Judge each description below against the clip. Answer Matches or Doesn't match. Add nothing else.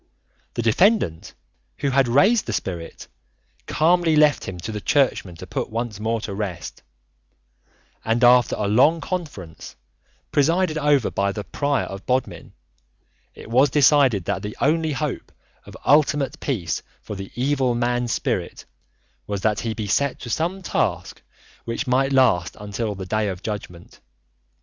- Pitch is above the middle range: Doesn't match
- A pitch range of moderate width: Doesn't match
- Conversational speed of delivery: Matches